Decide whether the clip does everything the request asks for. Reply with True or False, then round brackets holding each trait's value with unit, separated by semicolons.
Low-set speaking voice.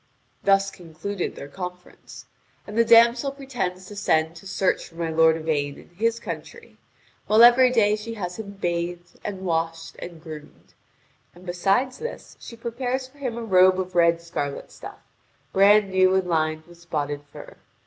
False (185 Hz)